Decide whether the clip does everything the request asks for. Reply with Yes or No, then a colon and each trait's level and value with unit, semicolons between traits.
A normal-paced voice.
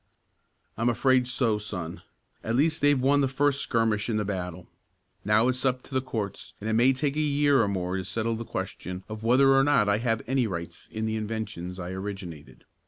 No: fast, 210 wpm